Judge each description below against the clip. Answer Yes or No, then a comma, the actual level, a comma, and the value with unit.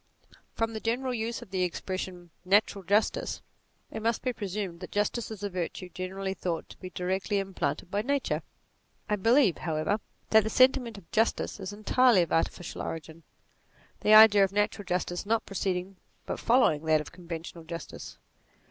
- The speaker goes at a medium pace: Yes, average, 170 wpm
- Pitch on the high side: Yes, high, 195 Hz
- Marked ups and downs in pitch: No, average, 3.6 semitones